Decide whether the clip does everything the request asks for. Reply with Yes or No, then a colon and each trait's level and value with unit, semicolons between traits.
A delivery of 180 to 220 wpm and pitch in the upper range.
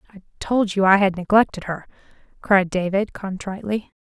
No: average, 150 wpm; high, 195 Hz